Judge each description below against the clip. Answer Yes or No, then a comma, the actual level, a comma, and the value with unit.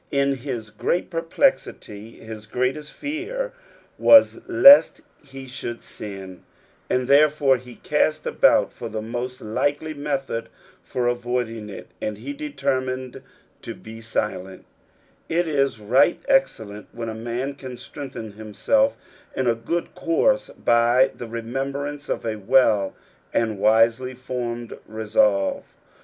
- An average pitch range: Yes, average, 4.4 semitones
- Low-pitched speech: Yes, low, 125 Hz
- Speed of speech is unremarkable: No, slow, 125 wpm